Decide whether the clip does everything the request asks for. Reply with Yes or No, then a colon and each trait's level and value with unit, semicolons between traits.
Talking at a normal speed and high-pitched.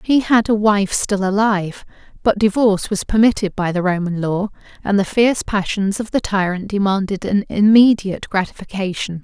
Yes: average, 160 wpm; high, 200 Hz